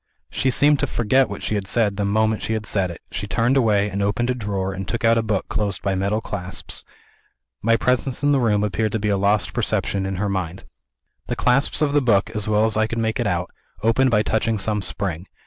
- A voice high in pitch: No, low, 105 Hz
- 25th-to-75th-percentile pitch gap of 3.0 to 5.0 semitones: No, narrow, 2.6 semitones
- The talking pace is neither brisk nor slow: No, fast, 240 wpm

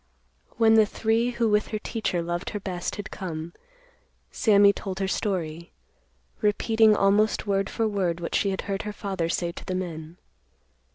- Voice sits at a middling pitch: No, high, 195 Hz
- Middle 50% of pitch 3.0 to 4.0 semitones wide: Yes, average, 3.5 semitones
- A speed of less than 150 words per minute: No, average, 170 wpm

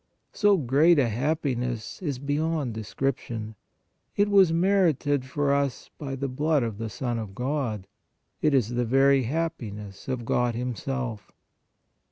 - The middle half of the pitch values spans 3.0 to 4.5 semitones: Yes, average, 4.2 semitones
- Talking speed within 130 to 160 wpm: Yes, average, 140 wpm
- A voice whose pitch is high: No, low, 135 Hz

